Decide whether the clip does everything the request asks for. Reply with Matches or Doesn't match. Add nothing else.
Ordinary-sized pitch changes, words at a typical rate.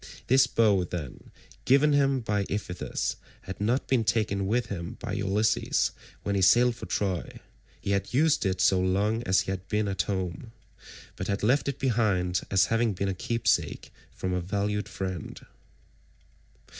Matches